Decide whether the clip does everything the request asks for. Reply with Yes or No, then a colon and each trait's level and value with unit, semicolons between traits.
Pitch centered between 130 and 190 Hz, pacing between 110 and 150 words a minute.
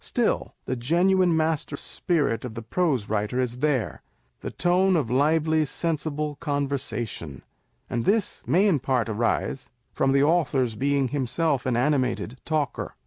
Yes: medium, 140 Hz; average, 140 wpm